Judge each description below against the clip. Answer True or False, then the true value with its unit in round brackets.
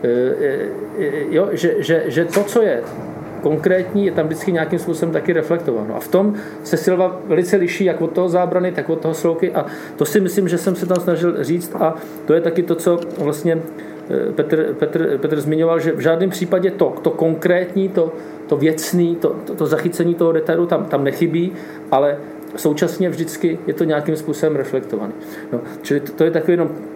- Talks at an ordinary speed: False (185 wpm)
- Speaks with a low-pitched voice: False (170 Hz)